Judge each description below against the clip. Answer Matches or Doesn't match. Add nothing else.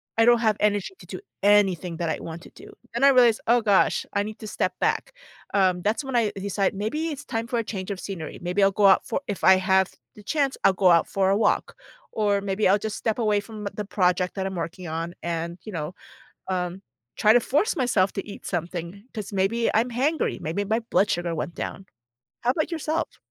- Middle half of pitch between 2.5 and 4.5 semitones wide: Matches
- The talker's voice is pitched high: Matches